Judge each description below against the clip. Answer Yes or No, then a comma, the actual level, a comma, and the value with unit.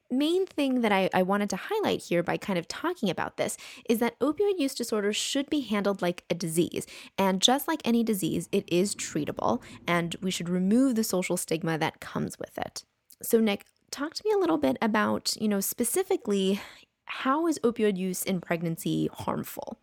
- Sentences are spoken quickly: No, average, 195 wpm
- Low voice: No, high, 215 Hz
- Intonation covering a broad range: Yes, wide, 6.7 semitones